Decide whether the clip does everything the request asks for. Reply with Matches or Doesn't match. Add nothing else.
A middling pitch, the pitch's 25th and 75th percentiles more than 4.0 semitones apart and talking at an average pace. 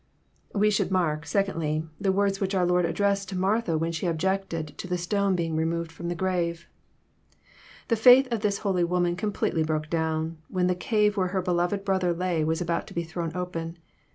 Doesn't match